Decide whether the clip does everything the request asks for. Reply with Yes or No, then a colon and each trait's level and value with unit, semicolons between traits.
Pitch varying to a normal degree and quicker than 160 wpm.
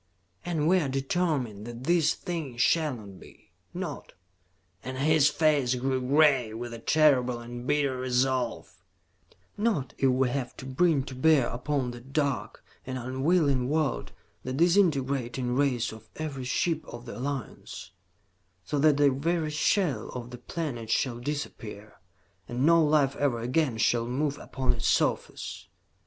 No: average, 3.7 semitones; average, 150 wpm